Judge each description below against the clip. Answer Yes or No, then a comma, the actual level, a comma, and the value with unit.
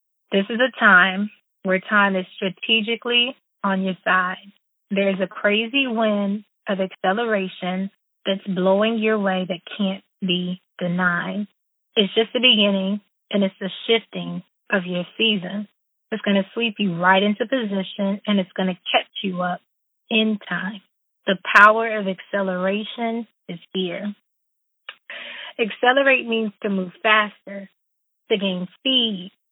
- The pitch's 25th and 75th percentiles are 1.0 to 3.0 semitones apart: Yes, narrow, 2.6 semitones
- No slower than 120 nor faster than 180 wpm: Yes, slow, 135 wpm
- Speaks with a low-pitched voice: No, high, 200 Hz